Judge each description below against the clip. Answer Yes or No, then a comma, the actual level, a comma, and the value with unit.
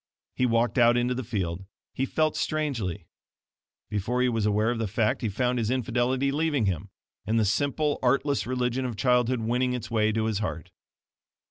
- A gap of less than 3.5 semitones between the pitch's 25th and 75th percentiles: Yes, average, 3.0 semitones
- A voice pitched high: No, low, 120 Hz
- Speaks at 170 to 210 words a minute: Yes, average, 185 wpm